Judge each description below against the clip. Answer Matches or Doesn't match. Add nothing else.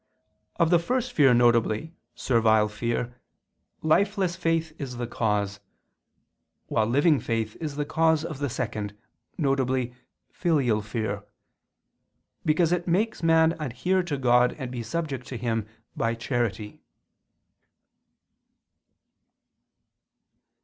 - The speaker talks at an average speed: Doesn't match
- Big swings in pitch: Matches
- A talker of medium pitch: Doesn't match